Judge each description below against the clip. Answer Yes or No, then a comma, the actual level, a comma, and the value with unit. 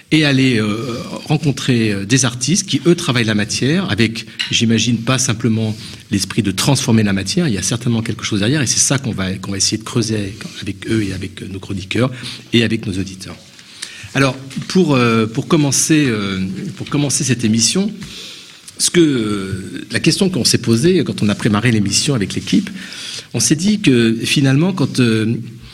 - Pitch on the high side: No, low, 120 Hz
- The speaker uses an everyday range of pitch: Yes, average, 4.3 semitones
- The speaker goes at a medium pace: Yes, average, 185 wpm